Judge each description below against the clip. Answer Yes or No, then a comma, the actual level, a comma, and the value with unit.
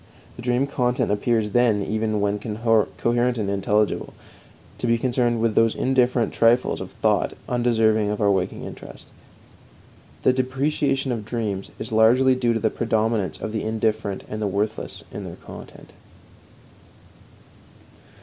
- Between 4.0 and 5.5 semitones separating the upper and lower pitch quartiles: No, narrow, 2.5 semitones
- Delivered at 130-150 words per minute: Yes, average, 140 wpm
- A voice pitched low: Yes, low, 115 Hz